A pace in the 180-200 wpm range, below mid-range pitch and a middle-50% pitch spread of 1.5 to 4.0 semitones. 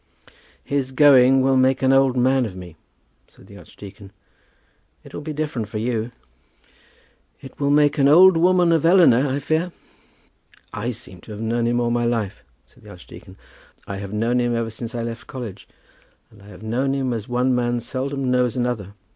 Yes: average, 190 wpm; low, 125 Hz; average, 3.2 semitones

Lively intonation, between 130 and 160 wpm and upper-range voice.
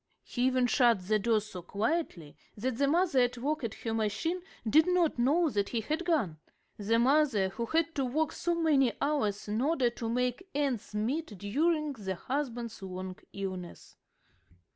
No: wide, 6.4 semitones; average, 170 wpm; high, 245 Hz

